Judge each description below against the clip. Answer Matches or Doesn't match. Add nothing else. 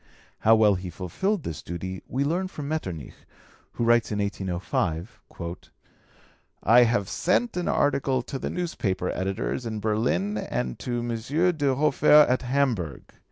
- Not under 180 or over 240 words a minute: Doesn't match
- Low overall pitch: Matches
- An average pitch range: Doesn't match